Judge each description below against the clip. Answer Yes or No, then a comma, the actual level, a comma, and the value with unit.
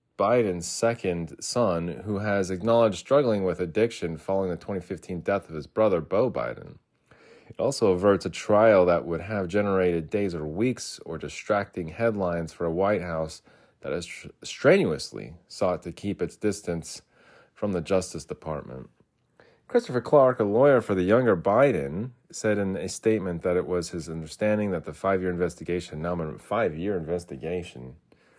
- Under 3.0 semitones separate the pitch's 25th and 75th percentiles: No, average, 3.5 semitones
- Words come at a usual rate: Yes, average, 160 wpm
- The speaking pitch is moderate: No, very low, 90 Hz